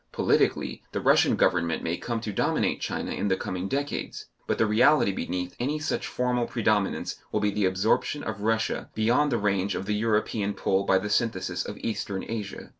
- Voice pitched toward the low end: Yes, low, 105 Hz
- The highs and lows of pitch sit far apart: No, average, 3.1 semitones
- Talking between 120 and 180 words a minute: No, average, 190 wpm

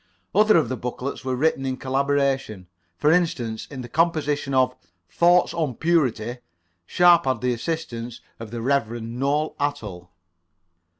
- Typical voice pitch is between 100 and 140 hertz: Yes, low, 135 Hz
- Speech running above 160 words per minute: No, average, 140 wpm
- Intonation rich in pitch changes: No, average, 4.6 semitones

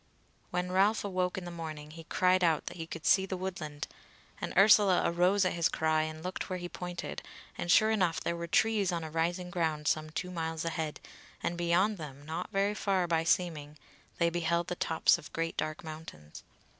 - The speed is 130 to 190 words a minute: No, average, 200 wpm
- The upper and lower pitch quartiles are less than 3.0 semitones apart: Yes, narrow, 2.4 semitones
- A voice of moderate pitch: Yes, medium, 170 Hz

